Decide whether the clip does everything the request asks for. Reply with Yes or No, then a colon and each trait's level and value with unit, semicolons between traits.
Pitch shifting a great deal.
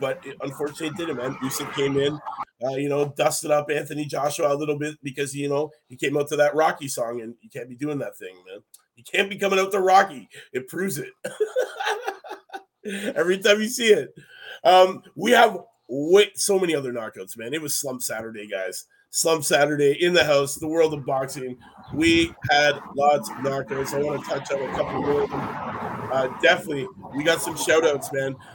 Yes: wide, 6.2 semitones